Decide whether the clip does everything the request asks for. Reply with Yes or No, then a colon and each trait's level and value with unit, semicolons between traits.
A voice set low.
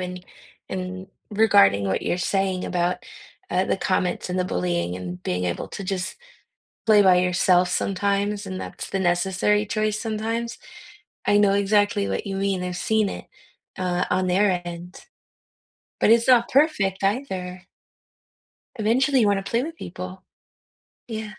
No: high, 190 Hz